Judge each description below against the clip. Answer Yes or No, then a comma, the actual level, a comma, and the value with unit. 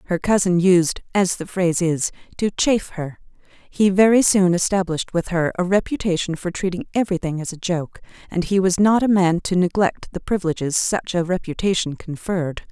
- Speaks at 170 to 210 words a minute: Yes, average, 180 wpm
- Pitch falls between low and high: Yes, medium, 180 Hz